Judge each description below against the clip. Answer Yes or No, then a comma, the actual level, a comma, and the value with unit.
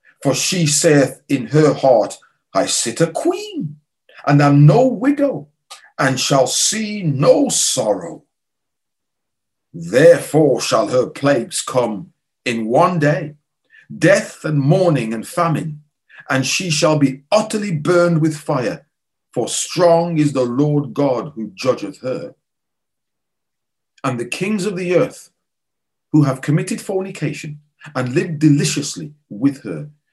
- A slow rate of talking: Yes, slow, 125 wpm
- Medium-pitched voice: Yes, medium, 150 Hz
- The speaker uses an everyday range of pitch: Yes, average, 3.7 semitones